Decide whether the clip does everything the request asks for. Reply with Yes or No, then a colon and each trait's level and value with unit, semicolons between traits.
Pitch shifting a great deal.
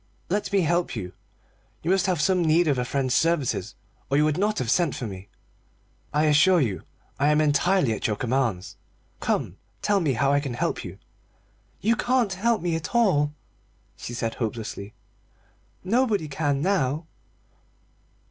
Yes: wide, 6.2 semitones